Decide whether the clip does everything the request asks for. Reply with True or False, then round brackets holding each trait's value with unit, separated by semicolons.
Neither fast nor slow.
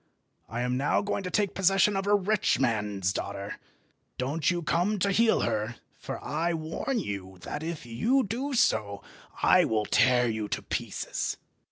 True (170 wpm)